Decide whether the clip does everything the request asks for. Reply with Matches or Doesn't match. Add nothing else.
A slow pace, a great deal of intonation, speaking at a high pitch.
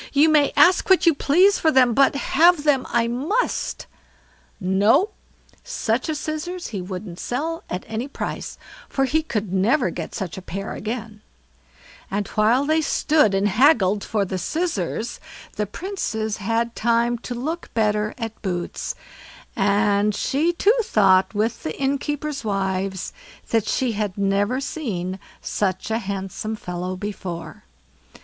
Doesn't match